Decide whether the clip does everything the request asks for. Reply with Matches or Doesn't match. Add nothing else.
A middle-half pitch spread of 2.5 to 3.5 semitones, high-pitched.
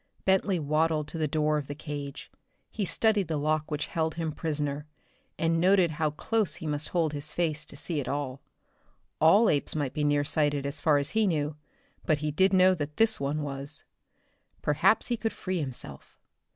Doesn't match